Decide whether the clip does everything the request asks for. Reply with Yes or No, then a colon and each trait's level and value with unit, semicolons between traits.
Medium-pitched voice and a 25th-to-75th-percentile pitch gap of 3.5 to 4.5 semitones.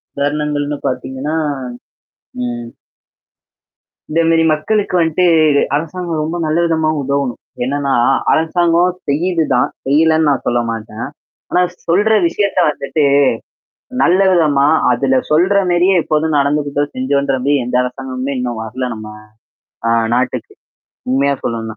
Yes: medium, 145 Hz; average, 3.8 semitones